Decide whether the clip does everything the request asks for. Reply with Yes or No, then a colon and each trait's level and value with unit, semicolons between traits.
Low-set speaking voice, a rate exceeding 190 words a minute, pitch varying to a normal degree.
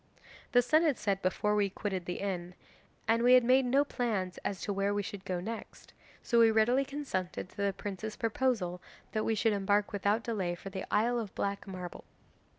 No: high, 205 Hz; average, 200 wpm; average, 3.5 semitones